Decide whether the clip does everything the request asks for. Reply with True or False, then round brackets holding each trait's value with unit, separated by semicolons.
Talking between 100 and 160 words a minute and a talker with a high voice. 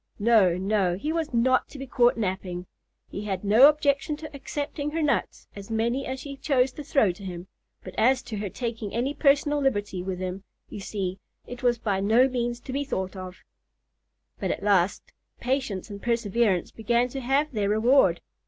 False (190 wpm; 235 Hz)